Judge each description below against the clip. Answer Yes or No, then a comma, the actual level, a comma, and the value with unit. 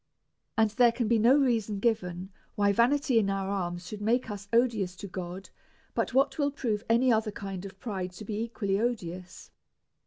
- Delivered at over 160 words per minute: Yes, average, 185 wpm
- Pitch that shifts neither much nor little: Yes, average, 3.4 semitones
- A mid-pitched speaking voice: No, high, 210 Hz